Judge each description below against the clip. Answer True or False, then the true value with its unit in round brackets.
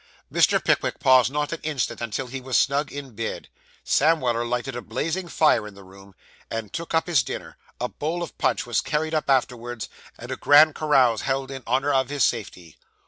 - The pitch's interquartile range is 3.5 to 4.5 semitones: True (3.9 semitones)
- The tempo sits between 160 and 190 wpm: False (200 wpm)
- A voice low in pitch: True (130 Hz)